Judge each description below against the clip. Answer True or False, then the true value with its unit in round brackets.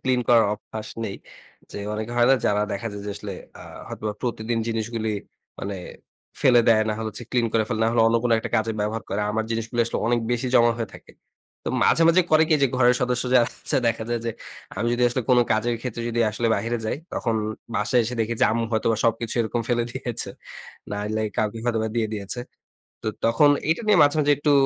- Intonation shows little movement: True (1.8 semitones)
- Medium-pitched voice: False (115 Hz)